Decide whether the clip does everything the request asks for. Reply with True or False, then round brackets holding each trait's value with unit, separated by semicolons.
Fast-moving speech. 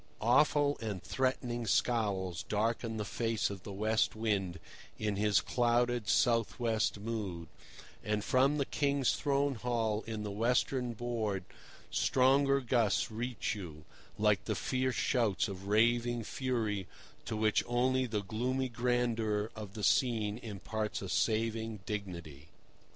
False (135 wpm)